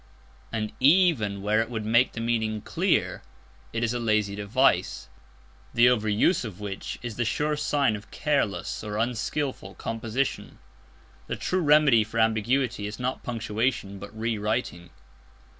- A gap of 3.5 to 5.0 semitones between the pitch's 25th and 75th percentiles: No, average, 3.1 semitones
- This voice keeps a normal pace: Yes, average, 150 wpm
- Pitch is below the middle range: Yes, low, 115 Hz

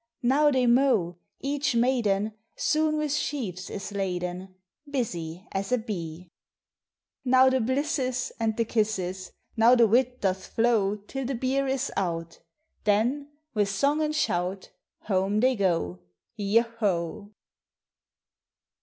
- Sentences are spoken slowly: Yes, slow, 125 wpm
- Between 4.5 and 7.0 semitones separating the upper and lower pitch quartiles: Yes, wide, 5.6 semitones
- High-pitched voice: Yes, high, 220 Hz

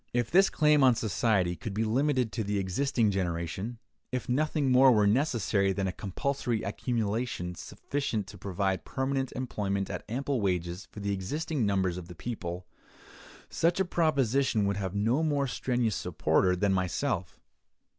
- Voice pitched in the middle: No, low, 110 Hz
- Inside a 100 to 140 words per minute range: No, average, 155 wpm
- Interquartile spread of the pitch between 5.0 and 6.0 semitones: Yes, wide, 5.6 semitones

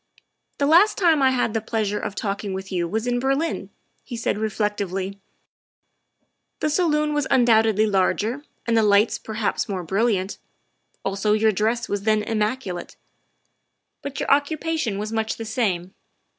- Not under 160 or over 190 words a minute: Yes, average, 180 wpm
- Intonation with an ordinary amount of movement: Yes, average, 4.4 semitones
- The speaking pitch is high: Yes, high, 220 Hz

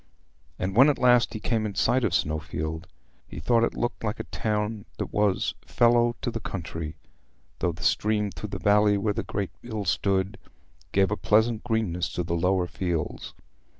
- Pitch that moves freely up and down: No, average, 3.8 semitones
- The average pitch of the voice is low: Yes, low, 105 Hz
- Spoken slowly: No, average, 185 wpm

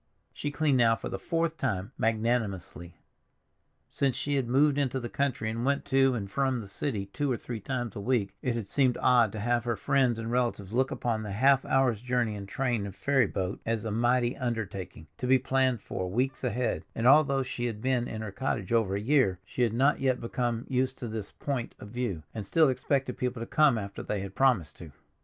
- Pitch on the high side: No, low, 120 Hz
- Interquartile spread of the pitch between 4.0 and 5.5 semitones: No, average, 3.5 semitones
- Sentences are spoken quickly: Yes, fast, 220 wpm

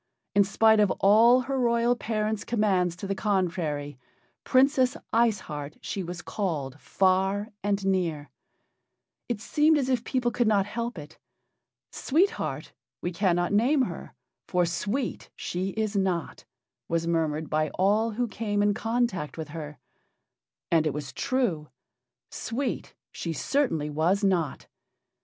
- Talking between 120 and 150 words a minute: Yes, average, 140 wpm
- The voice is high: Yes, high, 200 Hz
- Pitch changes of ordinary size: No, wide, 5.7 semitones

